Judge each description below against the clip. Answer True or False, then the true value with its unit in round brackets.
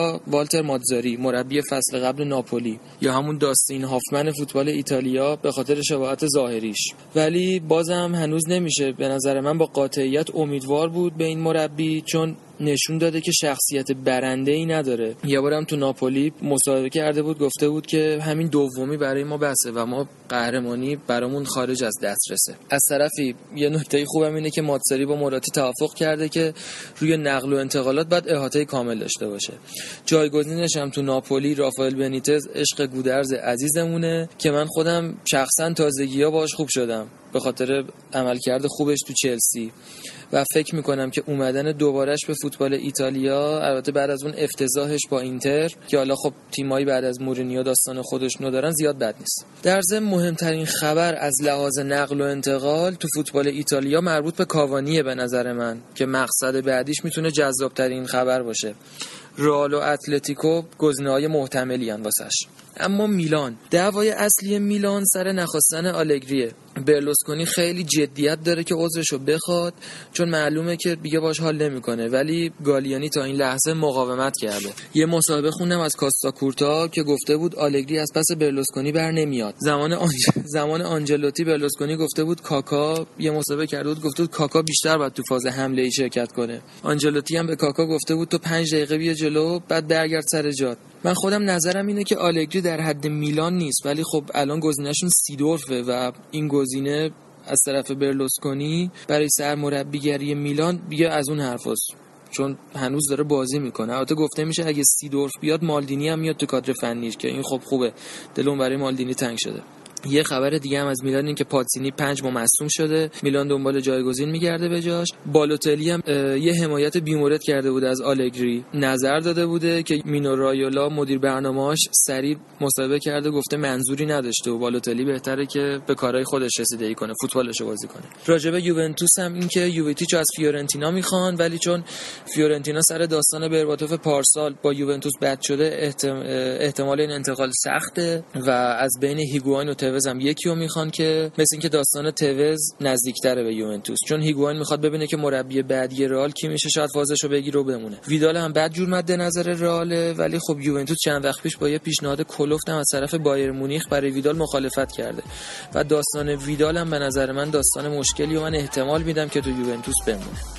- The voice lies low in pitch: False (145 Hz)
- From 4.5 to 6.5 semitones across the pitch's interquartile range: False (2.6 semitones)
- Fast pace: True (170 wpm)